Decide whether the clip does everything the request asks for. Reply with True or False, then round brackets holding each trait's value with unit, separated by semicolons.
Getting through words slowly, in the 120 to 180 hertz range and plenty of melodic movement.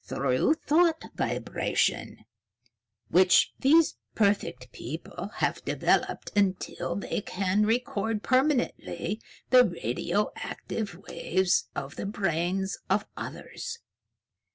False (90 wpm; 200 Hz; 5.7 semitones)